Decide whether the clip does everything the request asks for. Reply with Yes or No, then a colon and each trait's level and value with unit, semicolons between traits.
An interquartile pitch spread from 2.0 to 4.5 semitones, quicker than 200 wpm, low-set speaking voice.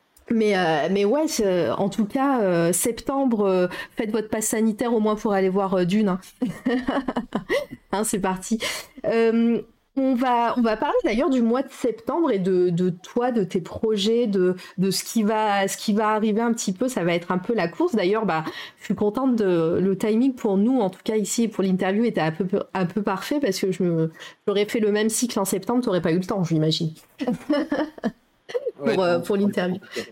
No: average, 4.0 semitones; average, 210 wpm; high, 215 Hz